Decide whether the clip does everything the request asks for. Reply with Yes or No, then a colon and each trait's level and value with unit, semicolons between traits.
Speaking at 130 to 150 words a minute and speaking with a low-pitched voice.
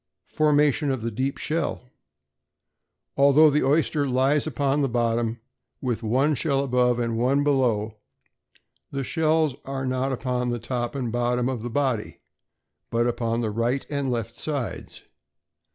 Yes: average, 145 wpm; low, 130 Hz